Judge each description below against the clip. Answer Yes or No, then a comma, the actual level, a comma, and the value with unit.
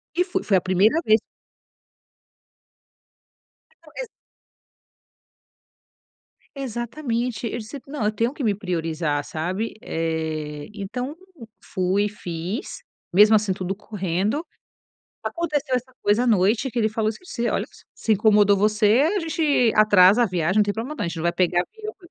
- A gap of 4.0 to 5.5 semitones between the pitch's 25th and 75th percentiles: Yes, average, 5.1 semitones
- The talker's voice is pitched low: No, high, 215 Hz